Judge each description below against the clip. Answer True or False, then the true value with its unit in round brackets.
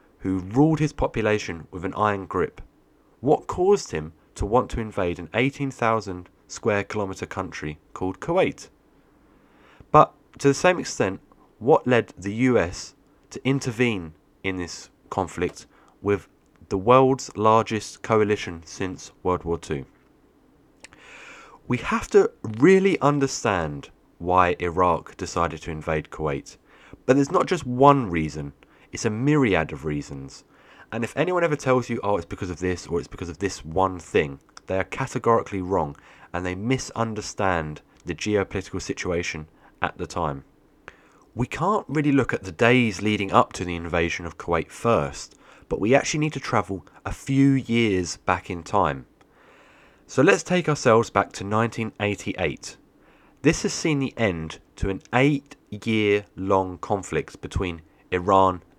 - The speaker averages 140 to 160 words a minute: True (150 wpm)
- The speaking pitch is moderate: False (100 Hz)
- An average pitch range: False (6.4 semitones)